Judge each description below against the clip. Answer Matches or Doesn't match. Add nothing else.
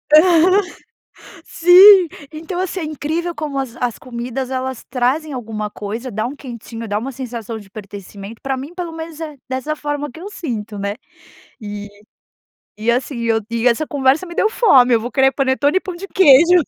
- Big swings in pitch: Matches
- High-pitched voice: Matches